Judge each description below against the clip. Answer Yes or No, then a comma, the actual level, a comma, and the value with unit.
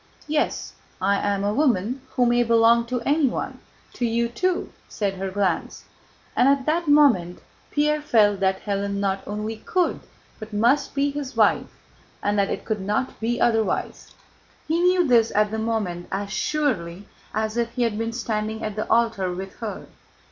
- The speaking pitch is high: Yes, high, 225 Hz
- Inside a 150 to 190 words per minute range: Yes, average, 170 wpm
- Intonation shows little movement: No, average, 4.2 semitones